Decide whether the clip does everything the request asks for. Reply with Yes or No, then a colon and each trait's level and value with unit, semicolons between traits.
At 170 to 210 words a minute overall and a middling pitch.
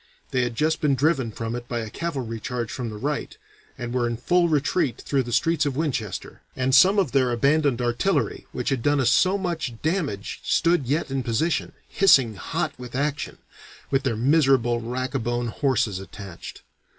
No: average, 185 wpm; low, 130 Hz